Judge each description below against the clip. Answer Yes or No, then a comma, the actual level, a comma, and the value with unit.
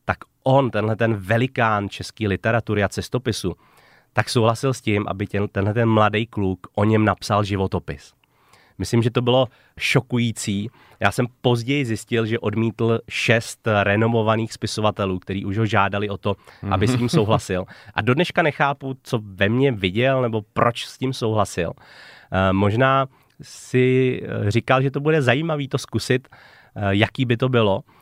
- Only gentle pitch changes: No, average, 3.8 semitones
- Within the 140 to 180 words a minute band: Yes, average, 155 wpm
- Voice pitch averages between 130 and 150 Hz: No, low, 115 Hz